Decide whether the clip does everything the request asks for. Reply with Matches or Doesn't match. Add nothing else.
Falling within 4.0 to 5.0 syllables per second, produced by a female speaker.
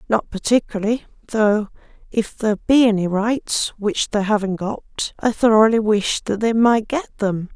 Matches